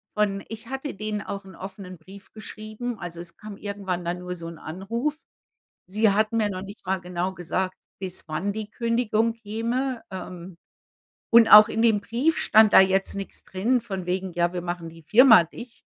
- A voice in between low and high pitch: No, high, 200 Hz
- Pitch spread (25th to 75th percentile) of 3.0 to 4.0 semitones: Yes, average, 3.5 semitones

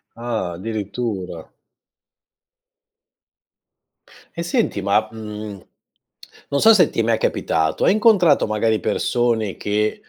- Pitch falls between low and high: No, low, 110 Hz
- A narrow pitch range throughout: No, average, 3.2 semitones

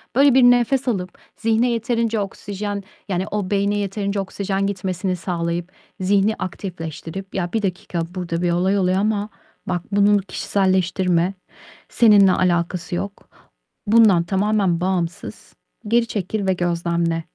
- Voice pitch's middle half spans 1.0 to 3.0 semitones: Yes, narrow, 2.6 semitones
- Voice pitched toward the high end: Yes, high, 195 Hz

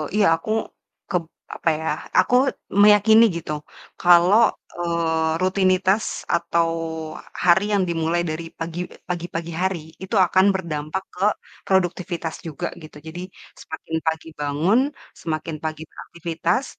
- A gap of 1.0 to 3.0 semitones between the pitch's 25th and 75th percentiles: Yes, narrow, 2.6 semitones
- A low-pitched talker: No, medium, 170 Hz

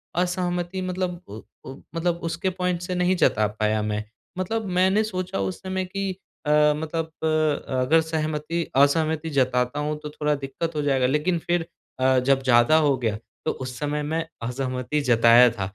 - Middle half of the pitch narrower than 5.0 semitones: No, average, 5.3 semitones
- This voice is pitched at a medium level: Yes, medium, 150 Hz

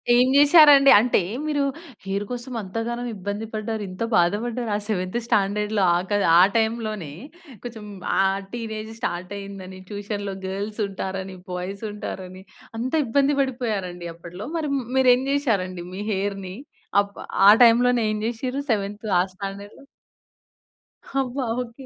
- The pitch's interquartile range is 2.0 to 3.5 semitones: No, average, 3.9 semitones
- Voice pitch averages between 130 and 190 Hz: No, high, 210 Hz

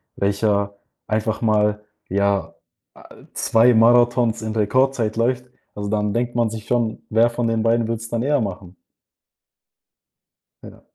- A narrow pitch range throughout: Yes, narrow, 2.1 semitones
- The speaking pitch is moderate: No, low, 110 Hz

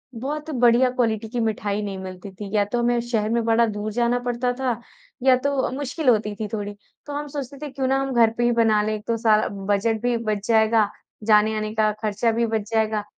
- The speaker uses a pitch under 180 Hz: No, high, 225 Hz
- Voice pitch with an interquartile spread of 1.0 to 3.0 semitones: Yes, narrow, 2.4 semitones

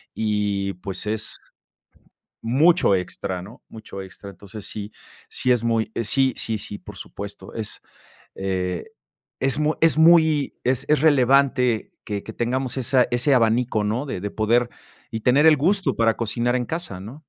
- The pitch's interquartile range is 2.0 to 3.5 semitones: No, average, 4.6 semitones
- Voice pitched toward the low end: Yes, low, 115 Hz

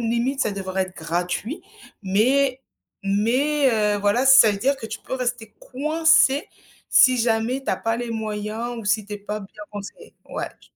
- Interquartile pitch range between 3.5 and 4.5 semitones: Yes, average, 4.1 semitones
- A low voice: No, high, 225 Hz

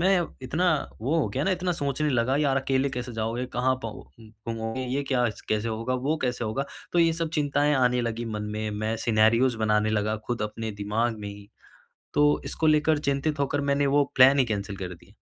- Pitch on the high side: No, low, 125 Hz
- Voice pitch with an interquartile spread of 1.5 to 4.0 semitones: No, average, 4.4 semitones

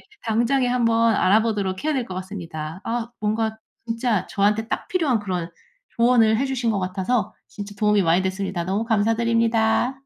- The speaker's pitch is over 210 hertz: Yes, high, 220 Hz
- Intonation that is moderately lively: Yes, average, 3.2 semitones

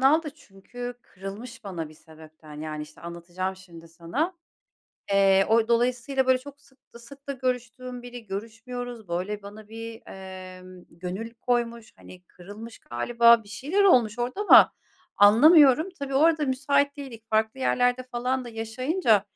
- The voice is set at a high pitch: Yes, high, 230 Hz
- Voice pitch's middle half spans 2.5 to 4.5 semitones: No, average, 4.9 semitones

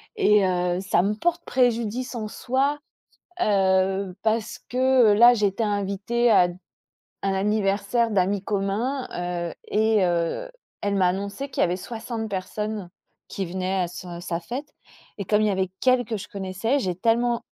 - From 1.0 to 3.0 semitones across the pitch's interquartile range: No, average, 3.7 semitones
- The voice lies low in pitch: No, high, 210 Hz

